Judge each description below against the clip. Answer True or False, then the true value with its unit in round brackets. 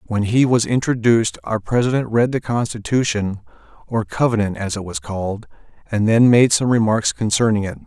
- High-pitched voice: False (115 Hz)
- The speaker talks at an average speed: True (170 wpm)